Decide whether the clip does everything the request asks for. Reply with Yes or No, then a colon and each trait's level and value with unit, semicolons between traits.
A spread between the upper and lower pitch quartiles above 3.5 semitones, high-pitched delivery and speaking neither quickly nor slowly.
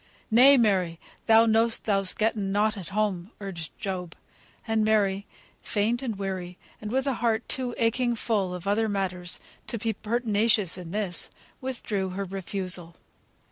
No: average, 3.1 semitones; high, 205 Hz; average, 150 wpm